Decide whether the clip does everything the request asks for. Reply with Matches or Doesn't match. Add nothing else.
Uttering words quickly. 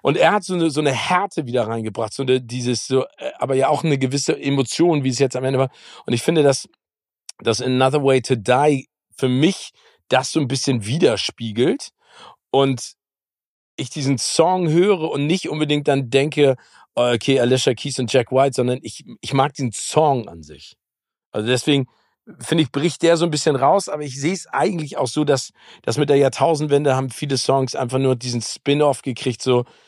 Matches